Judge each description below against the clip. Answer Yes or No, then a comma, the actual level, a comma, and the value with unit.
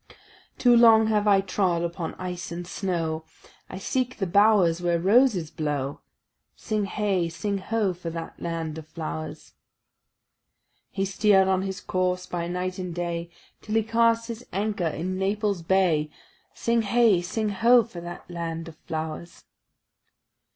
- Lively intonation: No, average, 3.7 semitones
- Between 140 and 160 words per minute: Yes, average, 150 wpm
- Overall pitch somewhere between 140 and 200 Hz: Yes, medium, 185 Hz